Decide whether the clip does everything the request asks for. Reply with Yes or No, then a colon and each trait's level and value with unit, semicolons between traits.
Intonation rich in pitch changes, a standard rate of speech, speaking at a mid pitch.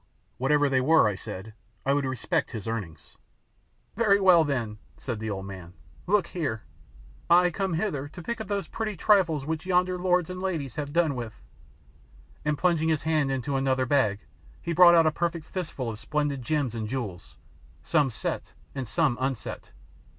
Yes: wide, 6.0 semitones; average, 175 wpm; medium, 145 Hz